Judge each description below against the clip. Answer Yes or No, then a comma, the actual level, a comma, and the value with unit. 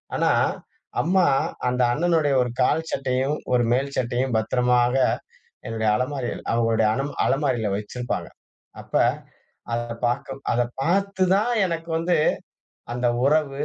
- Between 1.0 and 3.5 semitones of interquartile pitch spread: No, average, 4.5 semitones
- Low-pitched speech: Yes, low, 130 Hz